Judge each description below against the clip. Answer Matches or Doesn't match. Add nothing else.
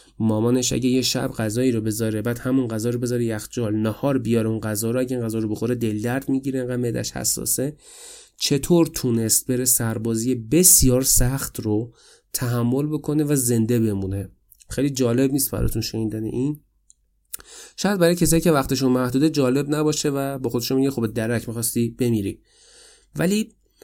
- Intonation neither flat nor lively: Matches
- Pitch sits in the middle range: Doesn't match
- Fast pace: Matches